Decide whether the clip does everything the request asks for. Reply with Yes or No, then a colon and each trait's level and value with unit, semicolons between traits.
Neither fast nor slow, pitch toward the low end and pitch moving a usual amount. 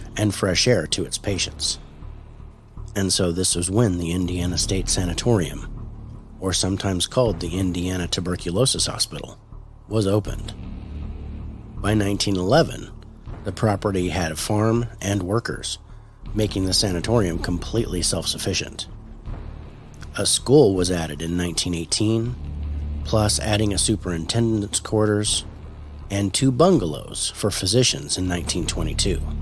No: slow, 115 wpm; very low, 95 Hz; average, 3.8 semitones